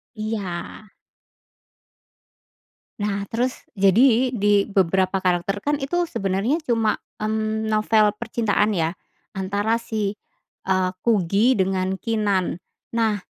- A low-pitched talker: No, high, 210 Hz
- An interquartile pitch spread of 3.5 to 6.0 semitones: No, average, 2.8 semitones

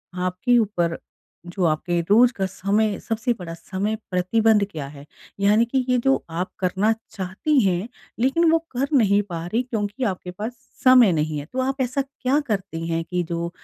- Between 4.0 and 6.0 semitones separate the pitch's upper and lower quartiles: Yes, wide, 5.6 semitones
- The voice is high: Yes, high, 205 Hz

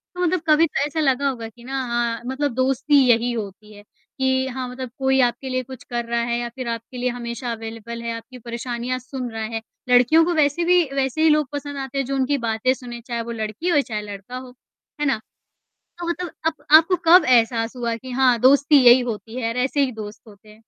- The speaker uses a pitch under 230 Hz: No, very high, 250 Hz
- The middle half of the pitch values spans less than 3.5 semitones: Yes, average, 2.8 semitones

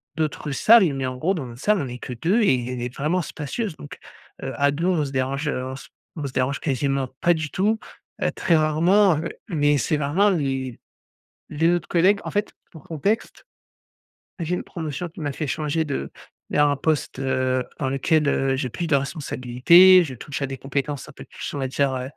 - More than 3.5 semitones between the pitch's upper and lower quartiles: Yes, average, 4.0 semitones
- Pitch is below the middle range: No, medium, 145 Hz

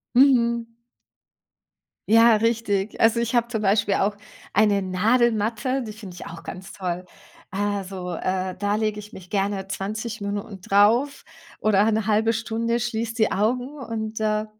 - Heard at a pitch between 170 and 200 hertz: No, high, 215 Hz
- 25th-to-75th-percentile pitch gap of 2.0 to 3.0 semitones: Yes, narrow, 2.6 semitones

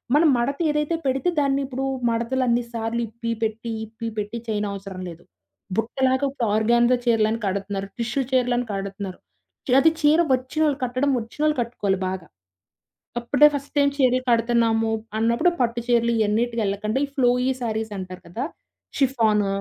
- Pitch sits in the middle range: No, high, 235 Hz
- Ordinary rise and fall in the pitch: Yes, average, 3.2 semitones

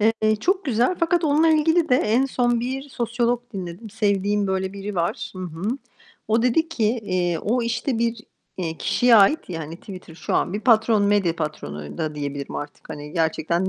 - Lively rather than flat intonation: Yes, wide, 5.8 semitones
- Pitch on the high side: Yes, high, 210 Hz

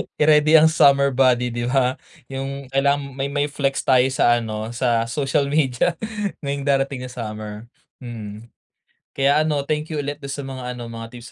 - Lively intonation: No, average, 2.8 semitones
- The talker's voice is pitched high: No, low, 135 Hz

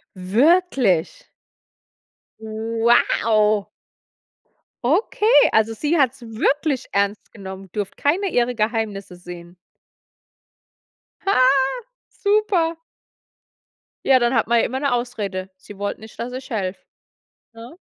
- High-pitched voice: Yes, high, 230 Hz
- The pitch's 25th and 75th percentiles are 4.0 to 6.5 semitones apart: Yes, average, 5.0 semitones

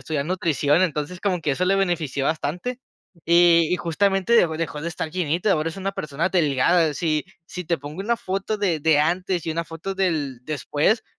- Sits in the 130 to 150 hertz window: No, medium, 170 Hz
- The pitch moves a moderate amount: Yes, average, 3.4 semitones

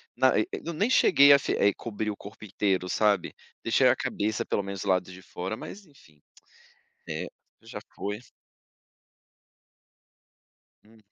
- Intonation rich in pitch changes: No, average, 3.5 semitones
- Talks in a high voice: No, low, 105 Hz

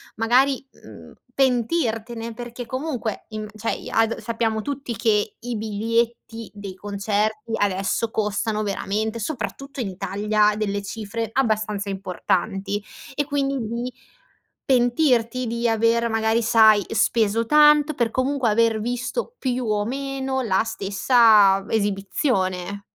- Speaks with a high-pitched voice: Yes, high, 225 Hz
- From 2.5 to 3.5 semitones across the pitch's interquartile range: Yes, average, 2.9 semitones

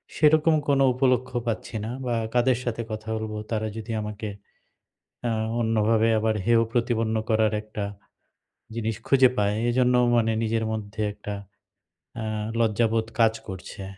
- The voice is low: Yes, low, 115 Hz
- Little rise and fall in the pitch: Yes, narrow, 1.9 semitones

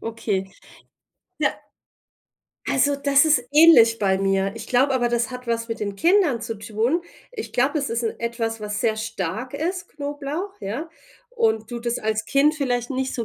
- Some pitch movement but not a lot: Yes, average, 4.2 semitones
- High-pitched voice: Yes, high, 240 Hz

